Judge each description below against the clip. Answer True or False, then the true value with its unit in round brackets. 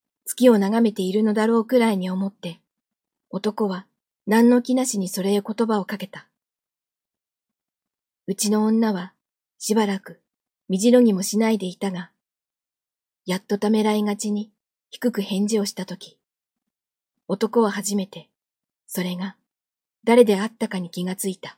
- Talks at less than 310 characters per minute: True (265 characters per minute)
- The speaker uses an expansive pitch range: False (2.9 semitones)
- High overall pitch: True (210 Hz)